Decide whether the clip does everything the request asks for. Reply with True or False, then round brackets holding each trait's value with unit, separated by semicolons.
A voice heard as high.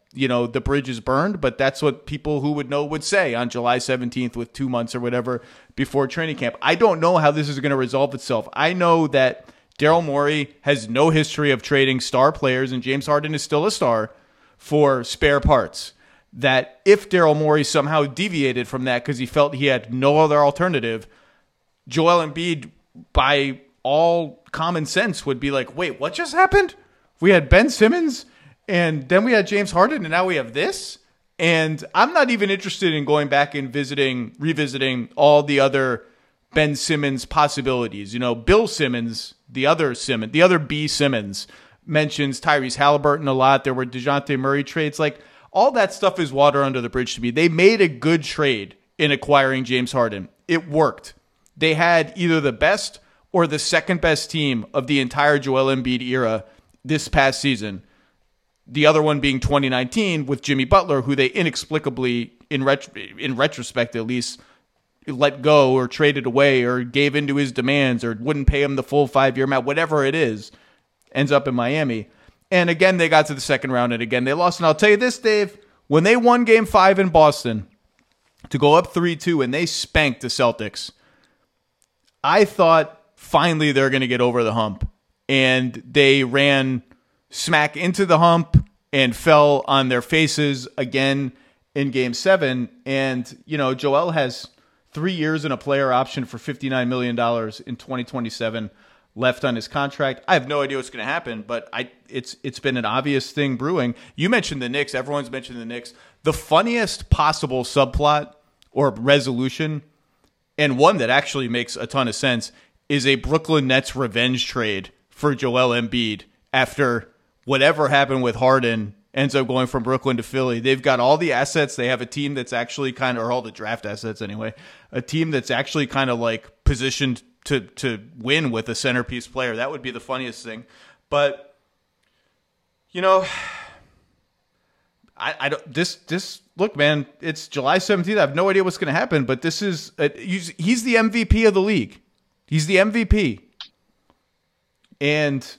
False (140 Hz)